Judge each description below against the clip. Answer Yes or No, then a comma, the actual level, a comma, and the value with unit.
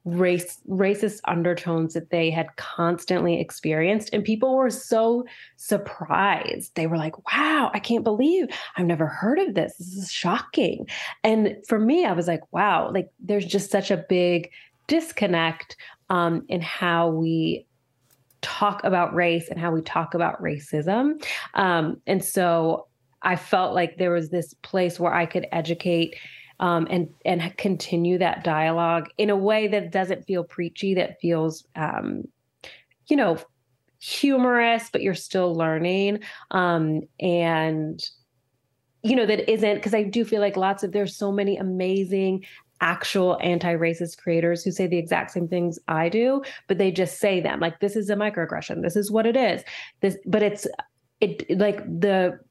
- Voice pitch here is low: No, medium, 180 Hz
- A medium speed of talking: Yes, average, 160 wpm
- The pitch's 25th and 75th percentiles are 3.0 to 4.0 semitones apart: Yes, average, 3.5 semitones